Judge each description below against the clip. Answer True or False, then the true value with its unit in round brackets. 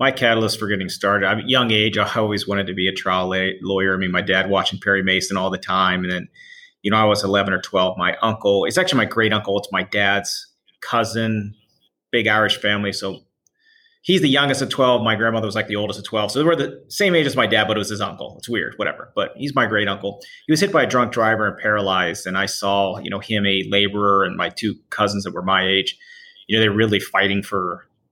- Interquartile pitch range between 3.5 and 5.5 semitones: False (2.7 semitones)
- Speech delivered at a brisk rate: True (250 wpm)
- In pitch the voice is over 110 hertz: False (105 Hz)